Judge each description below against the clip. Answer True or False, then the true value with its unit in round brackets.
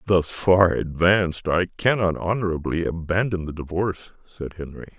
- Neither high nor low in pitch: False (90 Hz)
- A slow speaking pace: True (130 wpm)